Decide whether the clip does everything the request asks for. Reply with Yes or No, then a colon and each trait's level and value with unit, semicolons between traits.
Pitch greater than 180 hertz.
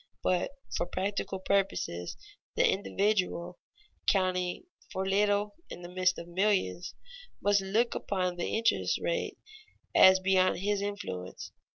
Yes: high, 190 Hz